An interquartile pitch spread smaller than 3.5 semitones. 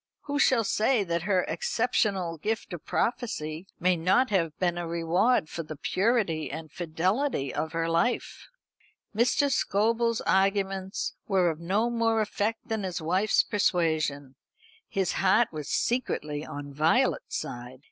No: average, 5.3 semitones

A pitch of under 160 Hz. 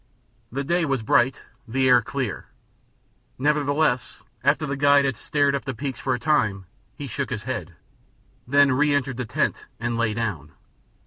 Yes: low, 135 Hz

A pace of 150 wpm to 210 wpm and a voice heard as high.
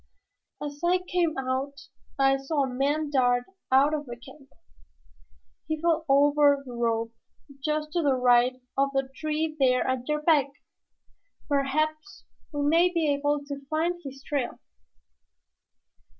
No: average, 140 wpm; very high, 285 Hz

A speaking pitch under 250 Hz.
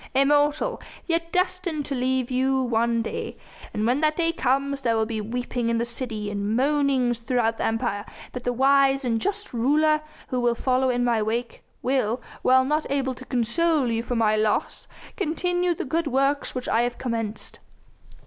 No: very high, 255 Hz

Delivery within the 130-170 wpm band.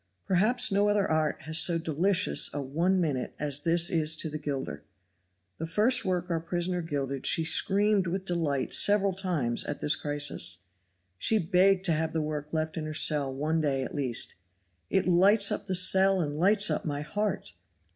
No: average, 185 wpm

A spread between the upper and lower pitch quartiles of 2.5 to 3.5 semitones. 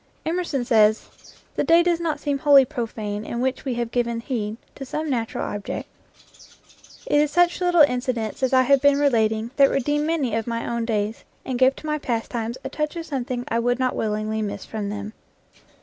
No: average, 4.3 semitones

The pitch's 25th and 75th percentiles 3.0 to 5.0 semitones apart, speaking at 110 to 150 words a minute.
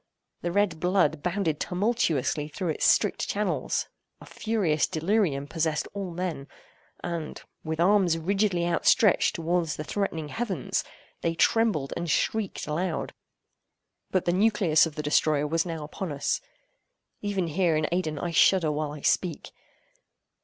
Yes: average, 3.8 semitones; average, 140 wpm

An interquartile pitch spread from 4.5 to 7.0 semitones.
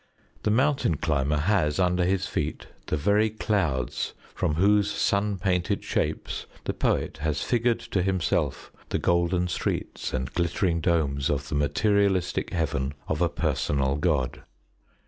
Yes: average, 5.1 semitones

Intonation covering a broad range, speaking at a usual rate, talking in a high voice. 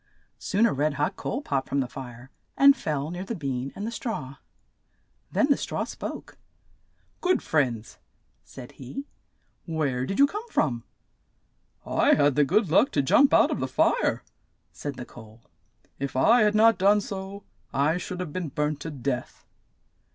No: wide, 7.6 semitones; average, 170 wpm; medium, 150 Hz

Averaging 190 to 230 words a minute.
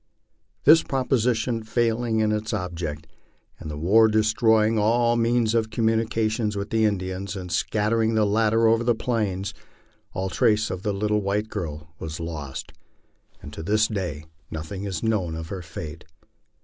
No: average, 155 wpm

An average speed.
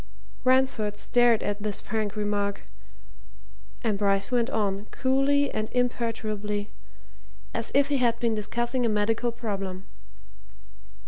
No: slow, 120 wpm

